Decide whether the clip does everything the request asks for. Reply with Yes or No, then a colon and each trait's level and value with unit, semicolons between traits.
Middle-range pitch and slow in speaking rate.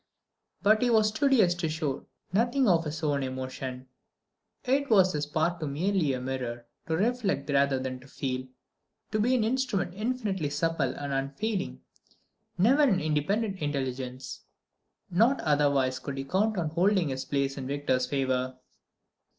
No: medium, 155 Hz; average, 155 wpm